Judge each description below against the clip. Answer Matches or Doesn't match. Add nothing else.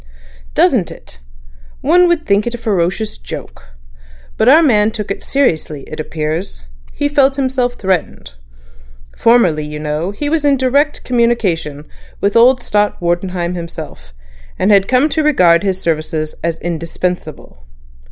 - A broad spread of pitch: Matches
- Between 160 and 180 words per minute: Doesn't match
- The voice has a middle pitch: Doesn't match